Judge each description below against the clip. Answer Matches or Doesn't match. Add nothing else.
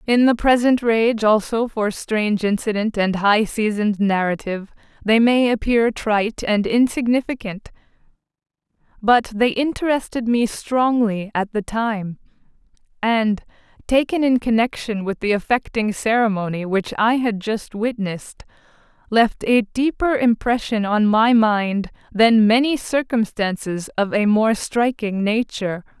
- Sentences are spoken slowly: Matches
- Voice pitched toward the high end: Matches